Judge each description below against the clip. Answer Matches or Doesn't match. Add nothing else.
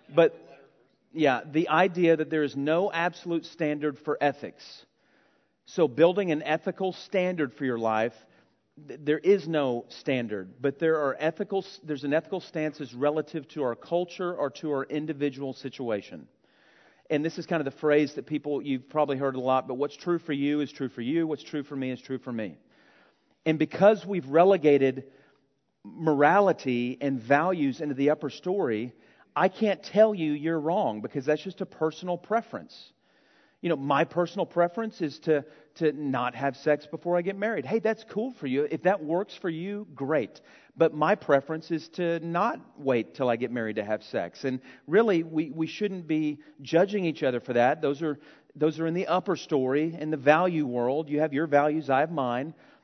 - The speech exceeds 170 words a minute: Matches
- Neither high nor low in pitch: Matches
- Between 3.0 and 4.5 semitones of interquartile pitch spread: Matches